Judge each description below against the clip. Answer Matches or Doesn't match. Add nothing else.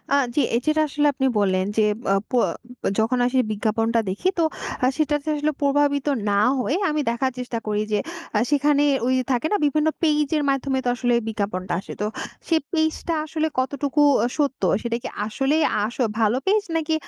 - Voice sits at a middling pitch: Doesn't match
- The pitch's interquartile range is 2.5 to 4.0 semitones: Doesn't match